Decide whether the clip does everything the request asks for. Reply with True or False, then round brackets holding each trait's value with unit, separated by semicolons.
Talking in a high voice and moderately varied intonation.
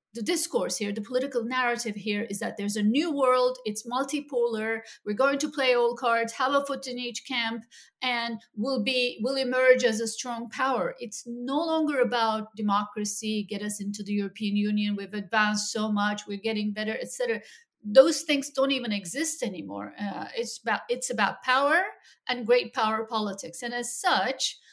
True (235 Hz; 3.4 semitones)